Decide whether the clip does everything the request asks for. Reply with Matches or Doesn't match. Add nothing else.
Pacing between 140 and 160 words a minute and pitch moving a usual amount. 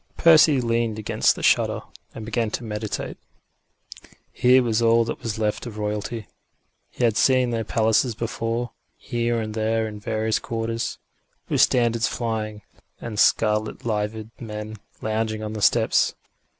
Doesn't match